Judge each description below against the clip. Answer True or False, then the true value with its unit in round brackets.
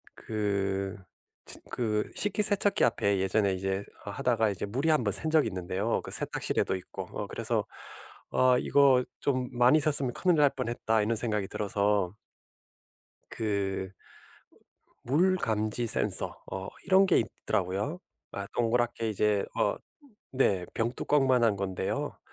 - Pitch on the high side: False (110 Hz)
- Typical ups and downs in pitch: True (4.7 semitones)